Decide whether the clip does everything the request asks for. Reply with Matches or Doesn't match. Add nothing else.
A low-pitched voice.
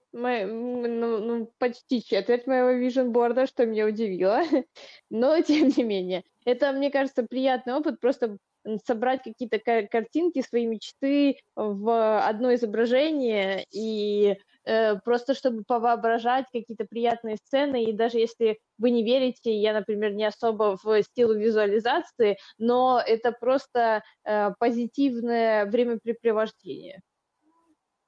Doesn't match